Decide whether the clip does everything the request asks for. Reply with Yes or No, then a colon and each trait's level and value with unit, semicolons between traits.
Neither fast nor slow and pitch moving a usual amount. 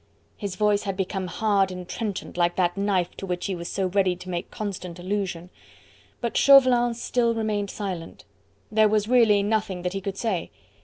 Yes: average, 185 wpm; average, 3.0 semitones